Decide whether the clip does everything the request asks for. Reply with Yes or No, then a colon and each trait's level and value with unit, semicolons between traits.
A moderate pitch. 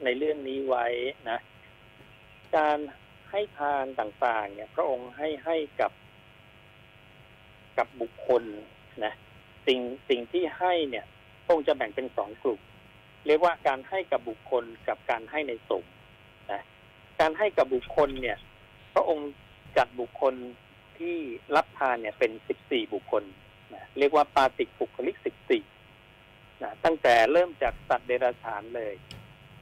No: low, 130 Hz